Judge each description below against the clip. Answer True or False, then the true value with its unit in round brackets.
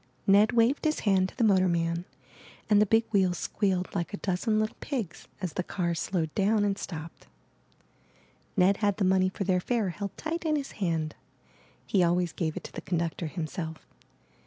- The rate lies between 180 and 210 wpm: True (185 wpm)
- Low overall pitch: False (190 Hz)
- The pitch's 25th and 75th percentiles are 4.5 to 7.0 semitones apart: False (3.6 semitones)